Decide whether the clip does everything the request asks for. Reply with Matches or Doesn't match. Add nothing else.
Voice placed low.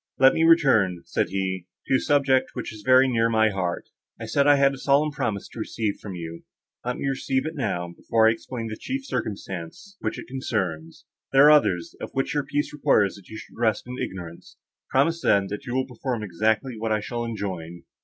Matches